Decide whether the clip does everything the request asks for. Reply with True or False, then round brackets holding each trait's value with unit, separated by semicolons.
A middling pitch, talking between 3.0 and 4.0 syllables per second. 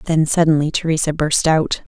False (155 Hz; 5.3 syllables/s)